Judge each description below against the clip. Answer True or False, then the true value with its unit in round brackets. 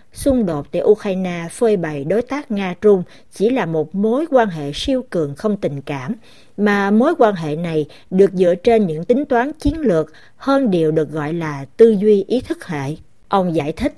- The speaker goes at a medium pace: True (195 wpm)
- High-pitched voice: True (195 Hz)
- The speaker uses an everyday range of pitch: False (6.7 semitones)